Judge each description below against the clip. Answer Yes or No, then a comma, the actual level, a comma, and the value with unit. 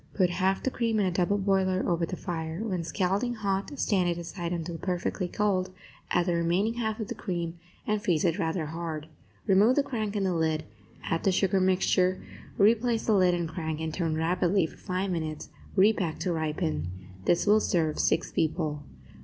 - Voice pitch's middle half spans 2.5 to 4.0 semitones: Yes, average, 3.1 semitones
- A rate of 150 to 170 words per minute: No, average, 190 wpm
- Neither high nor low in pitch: Yes, medium, 180 Hz